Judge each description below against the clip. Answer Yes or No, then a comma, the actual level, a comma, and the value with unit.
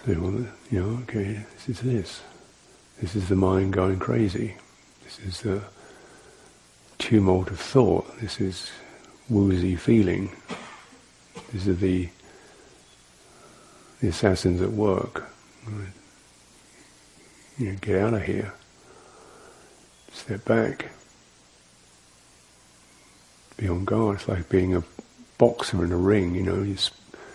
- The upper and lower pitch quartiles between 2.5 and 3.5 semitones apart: Yes, average, 3.1 semitones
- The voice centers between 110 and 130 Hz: No, very low, 95 Hz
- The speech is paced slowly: Yes, slow, 120 wpm